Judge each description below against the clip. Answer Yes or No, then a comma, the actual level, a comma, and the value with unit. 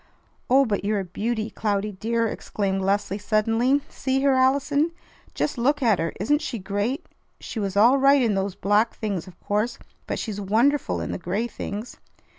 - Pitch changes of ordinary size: Yes, average, 4.5 semitones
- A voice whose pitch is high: Yes, high, 220 Hz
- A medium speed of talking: Yes, average, 180 wpm